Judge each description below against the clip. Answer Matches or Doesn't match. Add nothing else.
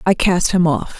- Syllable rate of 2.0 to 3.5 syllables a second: Doesn't match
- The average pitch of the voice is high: Doesn't match